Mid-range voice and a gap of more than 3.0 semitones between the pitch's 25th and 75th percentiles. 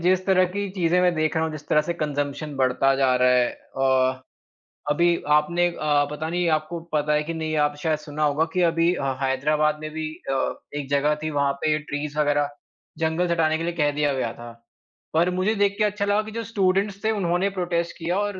Yes: medium, 160 Hz; average, 3.4 semitones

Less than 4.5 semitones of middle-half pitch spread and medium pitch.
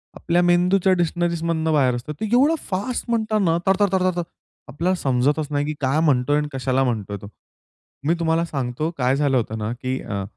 No: average, 5.2 semitones; medium, 155 Hz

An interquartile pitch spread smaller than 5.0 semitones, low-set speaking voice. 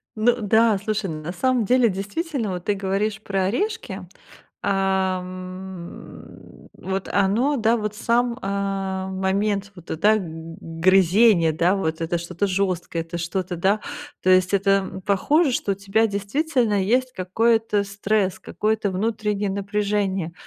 No: average, 2.7 semitones; high, 195 Hz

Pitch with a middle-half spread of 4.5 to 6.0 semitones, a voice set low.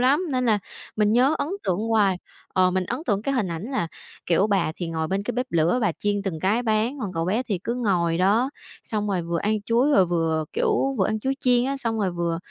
No: wide, 5.5 semitones; high, 205 Hz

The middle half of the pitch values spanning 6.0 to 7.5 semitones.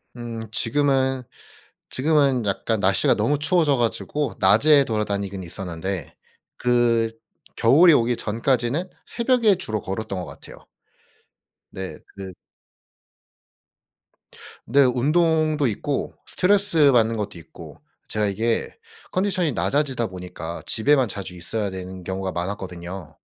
Yes: wide, 6.9 semitones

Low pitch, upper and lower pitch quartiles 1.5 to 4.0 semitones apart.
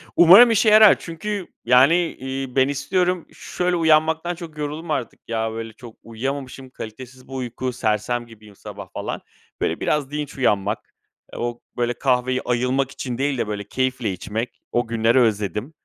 No: low, 130 Hz; average, 4.8 semitones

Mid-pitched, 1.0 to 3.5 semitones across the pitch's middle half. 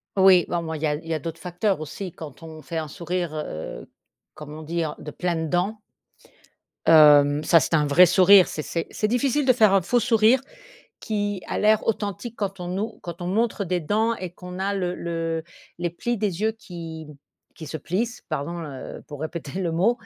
No: medium, 175 Hz; average, 4.1 semitones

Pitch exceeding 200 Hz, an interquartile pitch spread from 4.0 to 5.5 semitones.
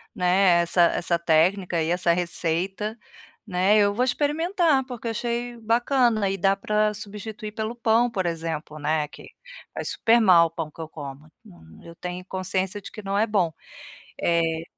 No: high, 195 Hz; average, 4.6 semitones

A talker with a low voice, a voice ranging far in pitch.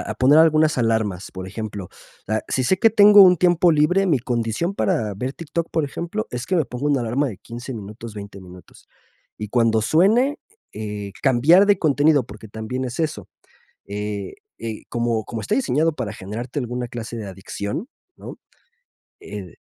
Yes: low, 120 Hz; wide, 6.7 semitones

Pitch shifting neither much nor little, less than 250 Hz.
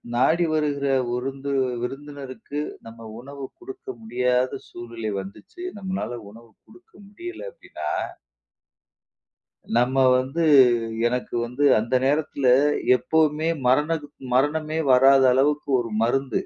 Yes: average, 3.8 semitones; medium, 140 Hz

